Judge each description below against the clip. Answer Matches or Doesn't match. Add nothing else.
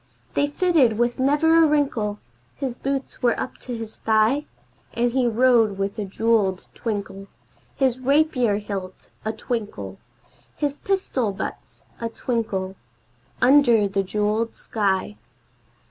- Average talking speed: Doesn't match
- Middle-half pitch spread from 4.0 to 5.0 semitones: Matches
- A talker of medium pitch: Doesn't match